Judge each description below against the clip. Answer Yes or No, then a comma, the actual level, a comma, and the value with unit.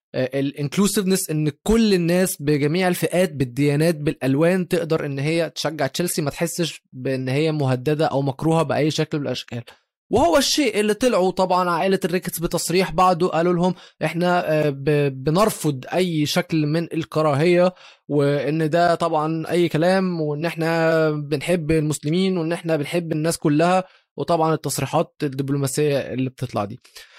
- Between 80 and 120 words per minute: No, fast, 135 wpm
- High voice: No, medium, 160 Hz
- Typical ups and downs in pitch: Yes, average, 3.2 semitones